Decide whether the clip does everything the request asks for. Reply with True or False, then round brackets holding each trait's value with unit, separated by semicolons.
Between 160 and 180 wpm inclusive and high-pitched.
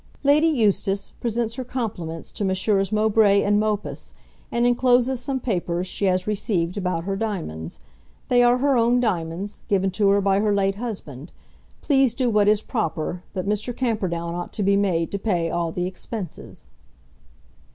True (165 wpm; 200 Hz)